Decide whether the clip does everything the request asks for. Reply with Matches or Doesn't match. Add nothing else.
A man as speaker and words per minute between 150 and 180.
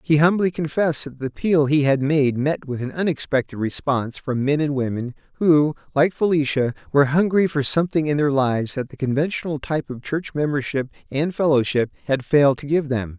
Doesn't match